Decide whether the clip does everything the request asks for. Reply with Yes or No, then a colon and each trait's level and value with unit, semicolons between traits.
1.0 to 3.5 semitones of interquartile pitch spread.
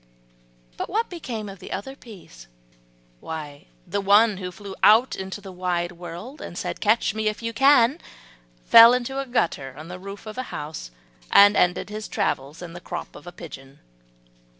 No: average, 4.8 semitones